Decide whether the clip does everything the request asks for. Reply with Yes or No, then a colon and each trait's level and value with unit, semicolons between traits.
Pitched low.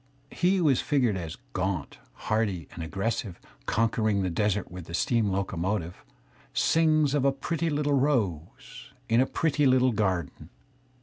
Yes: low, 110 Hz